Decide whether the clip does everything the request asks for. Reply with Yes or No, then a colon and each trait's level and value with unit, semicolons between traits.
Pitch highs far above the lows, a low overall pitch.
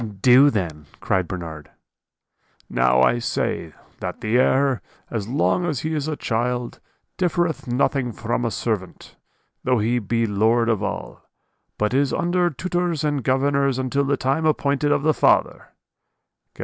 No: average, 4.4 semitones; low, 125 Hz